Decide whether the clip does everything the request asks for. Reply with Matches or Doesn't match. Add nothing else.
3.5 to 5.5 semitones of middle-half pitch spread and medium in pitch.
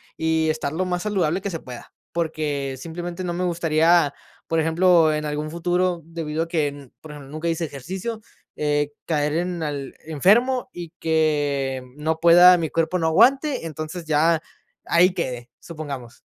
Doesn't match